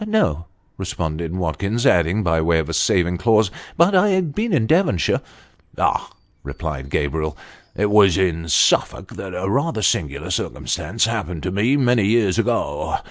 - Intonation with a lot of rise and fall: Yes, wide, 6.2 semitones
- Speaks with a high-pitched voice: No, very low, 95 Hz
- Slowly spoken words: No, average, 175 wpm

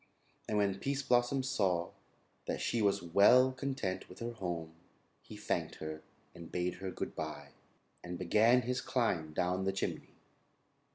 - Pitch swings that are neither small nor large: No, wide, 5.7 semitones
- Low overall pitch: Yes, very low, 95 Hz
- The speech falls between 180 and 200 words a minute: No, average, 155 wpm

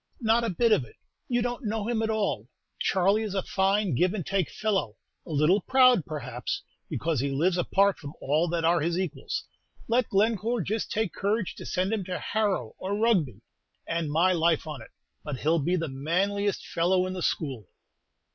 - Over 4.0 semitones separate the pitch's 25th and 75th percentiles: Yes, average, 4.9 semitones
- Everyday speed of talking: Yes, average, 195 wpm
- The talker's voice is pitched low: No, medium, 185 Hz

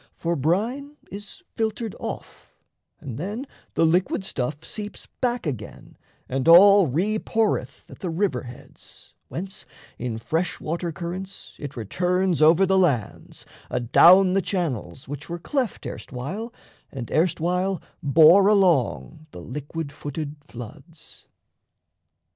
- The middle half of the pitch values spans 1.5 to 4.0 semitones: No, average, 5.3 semitones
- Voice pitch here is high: No, medium, 170 Hz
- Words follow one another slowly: Yes, slow, 125 wpm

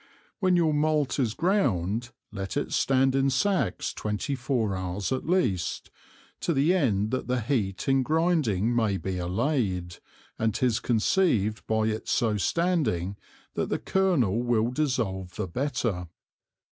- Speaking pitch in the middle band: No, low, 120 Hz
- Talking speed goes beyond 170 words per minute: No, average, 145 wpm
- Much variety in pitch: Yes, wide, 6.5 semitones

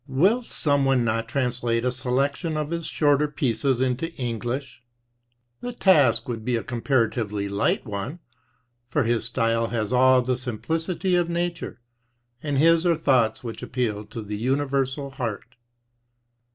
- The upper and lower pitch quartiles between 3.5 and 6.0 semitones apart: Yes, average, 4.1 semitones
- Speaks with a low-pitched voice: Yes, low, 130 Hz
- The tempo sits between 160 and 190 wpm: No, average, 145 wpm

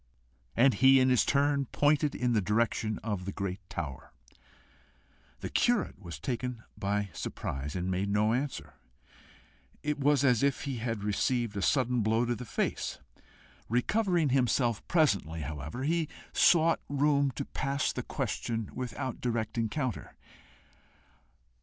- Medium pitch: No, low, 120 Hz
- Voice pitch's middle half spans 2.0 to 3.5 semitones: No, average, 5.2 semitones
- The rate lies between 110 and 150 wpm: Yes, average, 140 wpm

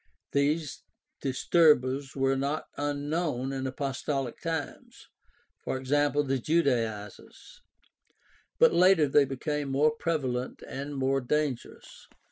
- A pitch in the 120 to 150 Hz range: Yes, medium, 140 Hz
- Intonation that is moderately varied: No, narrow, 2.2 semitones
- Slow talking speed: Yes, slow, 95 wpm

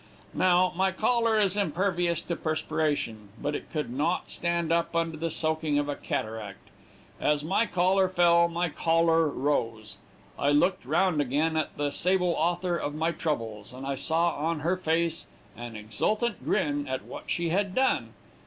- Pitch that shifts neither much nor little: Yes, average, 3.4 semitones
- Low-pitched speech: No, medium, 165 Hz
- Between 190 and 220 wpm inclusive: No, average, 165 wpm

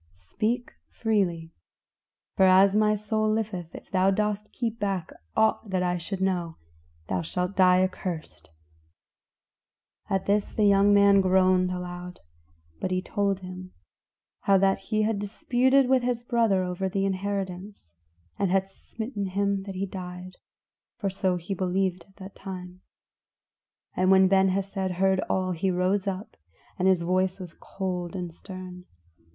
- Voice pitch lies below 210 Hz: Yes, high, 190 Hz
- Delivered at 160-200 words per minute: No, average, 150 wpm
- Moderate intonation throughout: No, narrow, 1.8 semitones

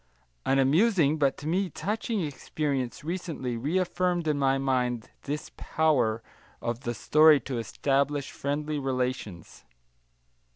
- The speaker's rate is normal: No, slow, 120 wpm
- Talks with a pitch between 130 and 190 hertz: Yes, medium, 140 Hz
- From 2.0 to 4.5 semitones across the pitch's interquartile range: Yes, average, 3.6 semitones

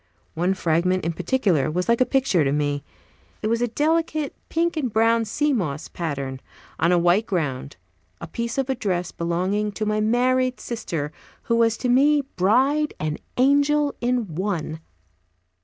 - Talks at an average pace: Yes, average, 165 wpm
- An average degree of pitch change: No, wide, 7.1 semitones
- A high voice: Yes, high, 215 Hz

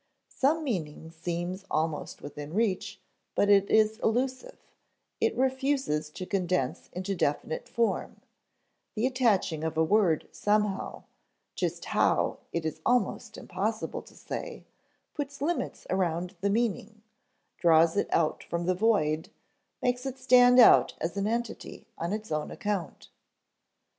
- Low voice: No, high, 200 Hz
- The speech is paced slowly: Yes, slow, 130 wpm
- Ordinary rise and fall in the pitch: No, wide, 6.0 semitones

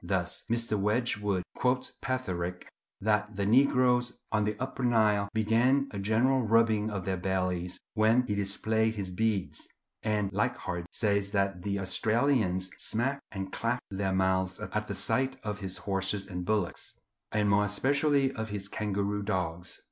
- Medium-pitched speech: No, low, 105 Hz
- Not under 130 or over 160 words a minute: Yes, average, 150 wpm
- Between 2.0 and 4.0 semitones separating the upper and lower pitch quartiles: Yes, average, 3.1 semitones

